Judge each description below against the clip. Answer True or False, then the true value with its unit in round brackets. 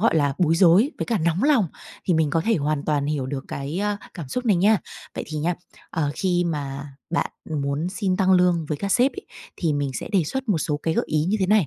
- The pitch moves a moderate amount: True (4.8 semitones)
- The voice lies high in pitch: False (170 Hz)